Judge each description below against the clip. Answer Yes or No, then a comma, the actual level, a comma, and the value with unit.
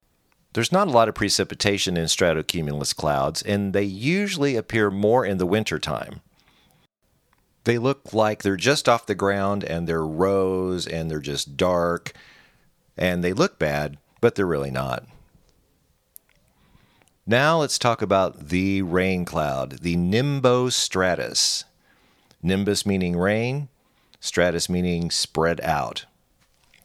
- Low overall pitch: Yes, very low, 95 Hz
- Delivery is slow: Yes, slow, 125 wpm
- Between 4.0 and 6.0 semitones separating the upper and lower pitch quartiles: Yes, average, 4.4 semitones